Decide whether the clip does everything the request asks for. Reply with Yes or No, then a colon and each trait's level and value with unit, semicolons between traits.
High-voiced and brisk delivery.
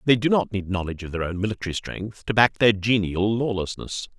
No: low, 105 Hz; fast, 215 wpm